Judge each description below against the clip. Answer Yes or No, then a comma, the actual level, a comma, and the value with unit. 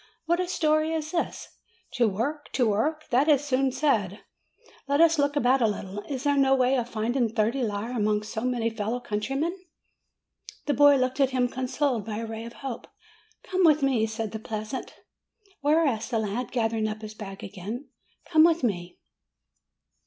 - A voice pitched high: Yes, very high, 250 Hz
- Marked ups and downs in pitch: No, average, 4.7 semitones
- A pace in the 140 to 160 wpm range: No, average, 180 wpm